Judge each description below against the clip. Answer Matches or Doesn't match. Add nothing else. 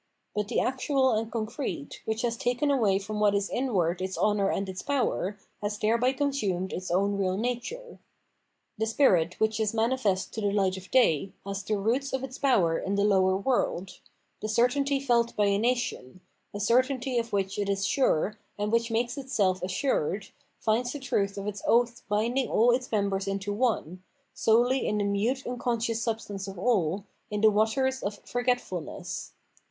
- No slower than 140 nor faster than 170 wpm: Doesn't match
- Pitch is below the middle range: Doesn't match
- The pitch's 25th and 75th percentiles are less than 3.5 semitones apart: Doesn't match